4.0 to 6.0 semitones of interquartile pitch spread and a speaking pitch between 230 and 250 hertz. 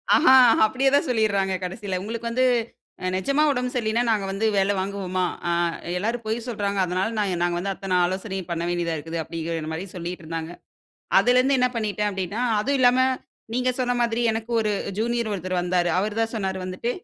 No: average, 4.4 semitones; high, 205 Hz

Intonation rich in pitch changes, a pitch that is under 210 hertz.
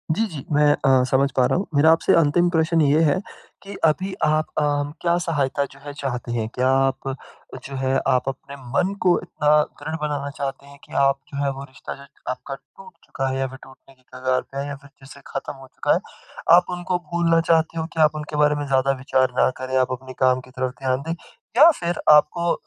No: average, 3.3 semitones; medium, 140 Hz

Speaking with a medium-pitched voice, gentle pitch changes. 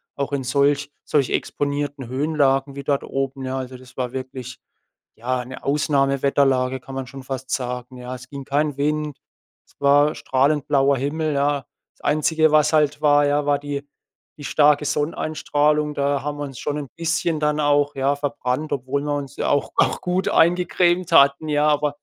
Yes: medium, 145 Hz; narrow, 1.7 semitones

